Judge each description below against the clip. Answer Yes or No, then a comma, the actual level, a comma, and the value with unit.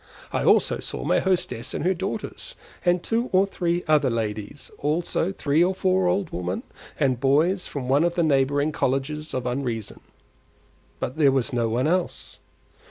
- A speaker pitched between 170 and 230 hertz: No, medium, 150 Hz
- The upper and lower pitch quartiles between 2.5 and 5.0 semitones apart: No, wide, 5.6 semitones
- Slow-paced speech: No, average, 170 wpm